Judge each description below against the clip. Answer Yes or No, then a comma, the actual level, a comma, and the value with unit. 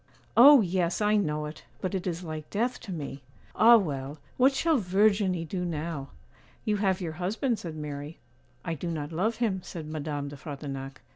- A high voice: No, medium, 175 Hz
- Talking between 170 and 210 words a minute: Yes, average, 185 wpm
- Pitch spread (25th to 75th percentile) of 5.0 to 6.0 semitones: Yes, wide, 5.5 semitones